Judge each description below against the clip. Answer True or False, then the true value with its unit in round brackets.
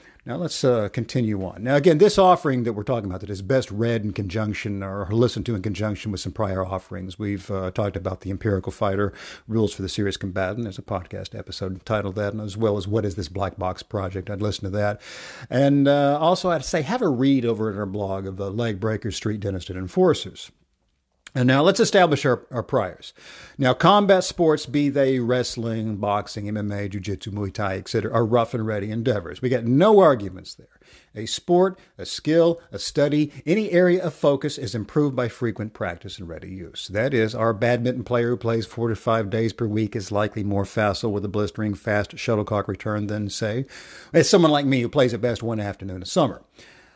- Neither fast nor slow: False (210 wpm)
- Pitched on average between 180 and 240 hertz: False (110 Hz)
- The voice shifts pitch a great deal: False (4.3 semitones)